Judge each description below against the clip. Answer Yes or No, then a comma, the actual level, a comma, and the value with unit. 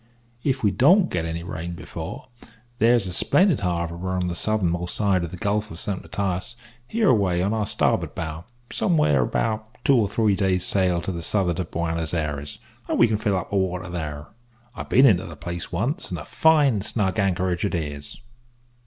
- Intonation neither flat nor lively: Yes, average, 4.1 semitones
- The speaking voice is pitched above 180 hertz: No, very low, 95 Hz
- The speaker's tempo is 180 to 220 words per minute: Yes, average, 190 wpm